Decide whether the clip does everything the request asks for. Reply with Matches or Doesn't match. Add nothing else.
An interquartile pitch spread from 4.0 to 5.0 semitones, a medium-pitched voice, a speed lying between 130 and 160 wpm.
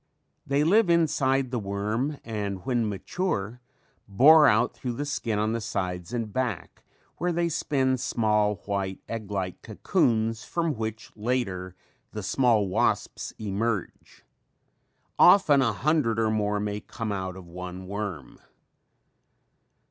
Doesn't match